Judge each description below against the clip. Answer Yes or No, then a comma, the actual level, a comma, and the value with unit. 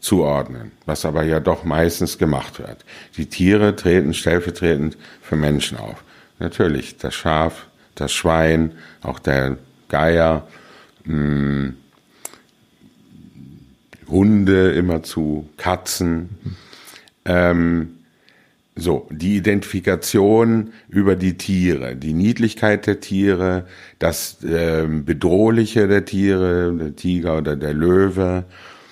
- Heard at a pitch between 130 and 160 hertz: No, very low, 85 Hz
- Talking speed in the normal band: No, slow, 95 wpm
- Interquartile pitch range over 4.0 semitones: No, average, 3.2 semitones